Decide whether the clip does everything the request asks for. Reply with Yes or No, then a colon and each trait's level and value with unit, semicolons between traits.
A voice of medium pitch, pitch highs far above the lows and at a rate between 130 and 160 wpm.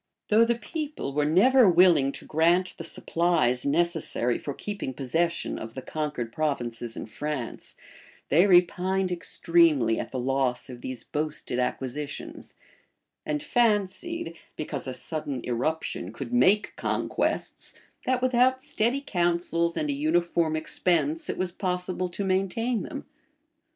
Yes: medium, 170 Hz; wide, 6.0 semitones; slow, 135 wpm